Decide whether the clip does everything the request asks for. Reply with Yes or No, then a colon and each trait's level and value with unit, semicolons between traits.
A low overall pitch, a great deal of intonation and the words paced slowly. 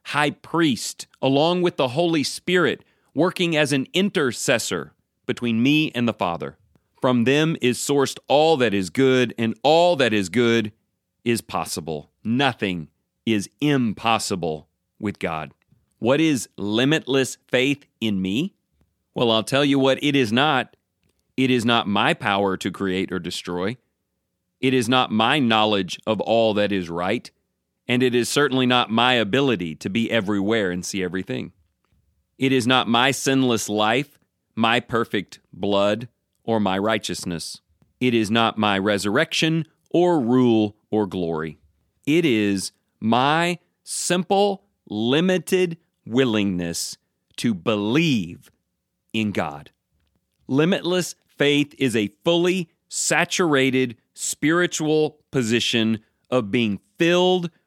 Yes: low, 115 Hz; wide, 5.7 semitones; slow, 130 wpm